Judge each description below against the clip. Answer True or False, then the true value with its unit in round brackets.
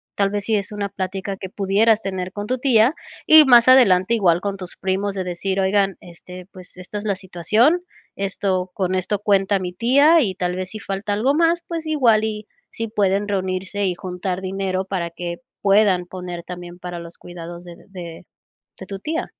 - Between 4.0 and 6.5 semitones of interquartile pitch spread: False (2.7 semitones)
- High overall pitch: True (195 Hz)